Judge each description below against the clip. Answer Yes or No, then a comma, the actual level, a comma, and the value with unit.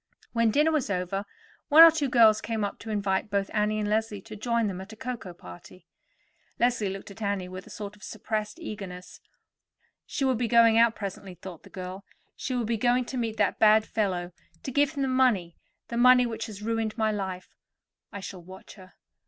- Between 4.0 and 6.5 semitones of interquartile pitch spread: No, average, 3.2 semitones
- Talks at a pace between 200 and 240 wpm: Yes, fast, 205 wpm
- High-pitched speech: Yes, high, 215 Hz